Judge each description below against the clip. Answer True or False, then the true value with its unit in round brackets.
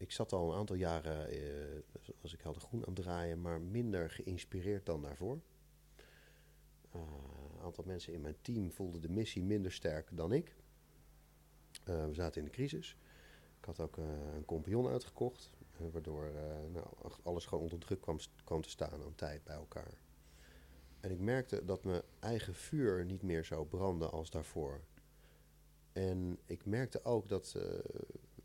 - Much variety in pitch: False (3.5 semitones)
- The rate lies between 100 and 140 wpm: False (175 wpm)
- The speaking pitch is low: True (85 Hz)